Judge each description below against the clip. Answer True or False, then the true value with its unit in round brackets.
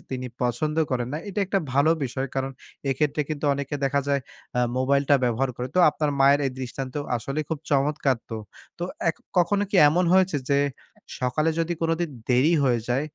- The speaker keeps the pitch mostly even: False (3.0 semitones)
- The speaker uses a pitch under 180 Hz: True (140 Hz)